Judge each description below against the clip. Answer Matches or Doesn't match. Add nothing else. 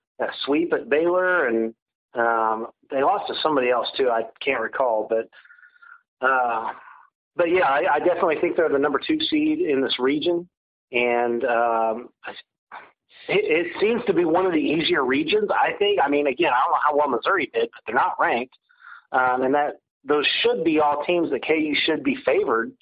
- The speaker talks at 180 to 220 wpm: Matches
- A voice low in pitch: Doesn't match